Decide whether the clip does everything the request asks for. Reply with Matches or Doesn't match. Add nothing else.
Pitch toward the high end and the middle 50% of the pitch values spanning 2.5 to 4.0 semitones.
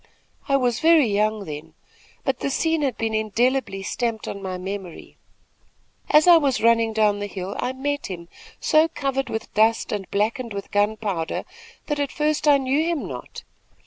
Doesn't match